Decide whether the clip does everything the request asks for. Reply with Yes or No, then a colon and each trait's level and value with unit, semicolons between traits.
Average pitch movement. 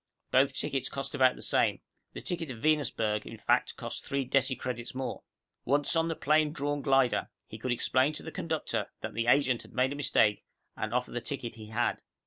Yes: average, 3.1 semitones